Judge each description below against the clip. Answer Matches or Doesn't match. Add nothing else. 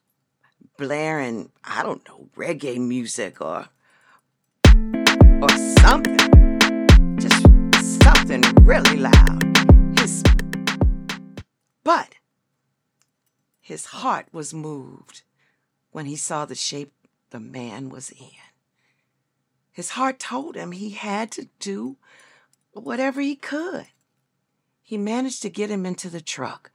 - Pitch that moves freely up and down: Matches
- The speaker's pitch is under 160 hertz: Doesn't match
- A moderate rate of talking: Doesn't match